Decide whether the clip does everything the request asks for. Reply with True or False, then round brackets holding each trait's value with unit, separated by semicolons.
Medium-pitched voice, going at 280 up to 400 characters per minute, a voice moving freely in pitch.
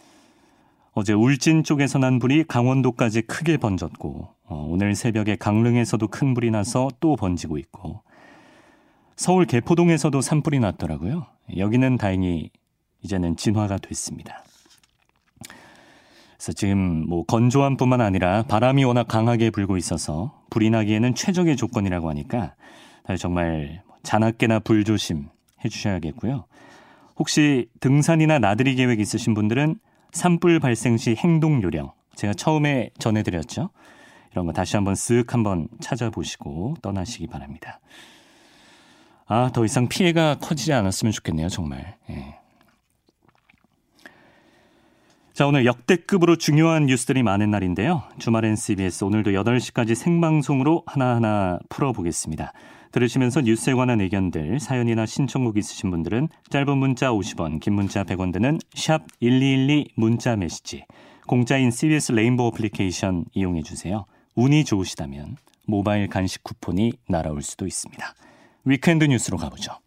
False (115 Hz; 310 characters per minute; 6.2 semitones)